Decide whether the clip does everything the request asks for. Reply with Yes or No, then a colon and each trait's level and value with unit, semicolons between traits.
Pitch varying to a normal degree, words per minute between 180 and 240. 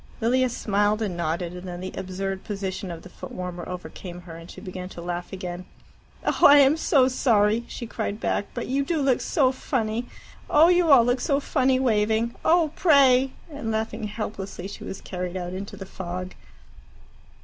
No: wide, 5.9 semitones; average, 185 wpm